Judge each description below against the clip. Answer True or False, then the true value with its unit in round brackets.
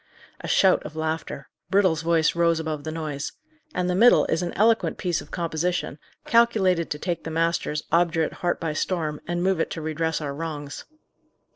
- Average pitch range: False (2.1 semitones)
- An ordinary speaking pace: True (185 wpm)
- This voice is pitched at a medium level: True (165 Hz)